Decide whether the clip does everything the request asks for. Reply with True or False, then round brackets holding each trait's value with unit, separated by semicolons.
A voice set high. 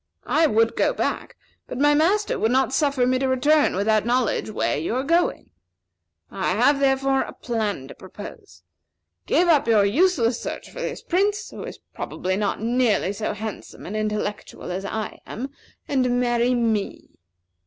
True (245 Hz)